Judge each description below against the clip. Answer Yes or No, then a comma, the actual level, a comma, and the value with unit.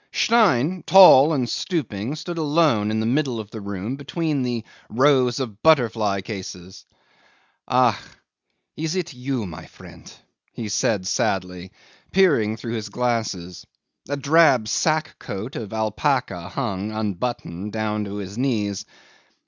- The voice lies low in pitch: Yes, low, 115 Hz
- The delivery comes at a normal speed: No, slow, 130 wpm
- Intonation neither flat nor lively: No, wide, 5.7 semitones